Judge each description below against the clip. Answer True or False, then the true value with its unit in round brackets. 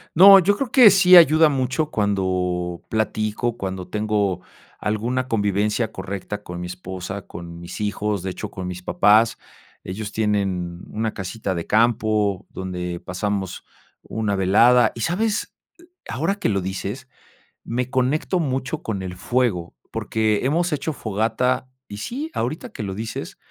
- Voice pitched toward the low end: True (105 Hz)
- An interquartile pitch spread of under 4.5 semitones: False (5.2 semitones)